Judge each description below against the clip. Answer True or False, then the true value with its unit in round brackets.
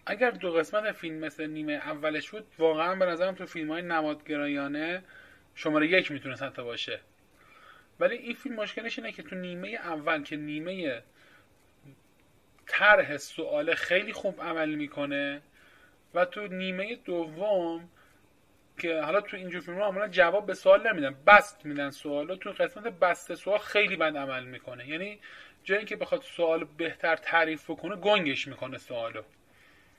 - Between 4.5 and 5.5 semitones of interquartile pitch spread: True (5.2 semitones)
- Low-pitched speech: False (170 Hz)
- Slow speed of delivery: False (150 wpm)